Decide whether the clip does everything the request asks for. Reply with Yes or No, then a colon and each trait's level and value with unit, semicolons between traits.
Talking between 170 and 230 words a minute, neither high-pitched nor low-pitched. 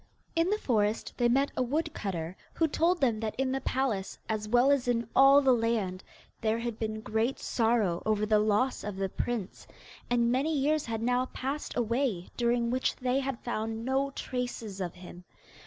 No: average, 185 wpm; high, 235 Hz